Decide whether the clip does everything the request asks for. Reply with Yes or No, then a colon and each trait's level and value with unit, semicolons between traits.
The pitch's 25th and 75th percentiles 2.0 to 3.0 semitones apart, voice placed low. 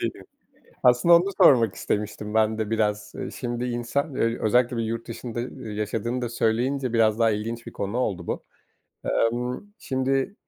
Yes: narrow, 2.4 semitones; low, 115 Hz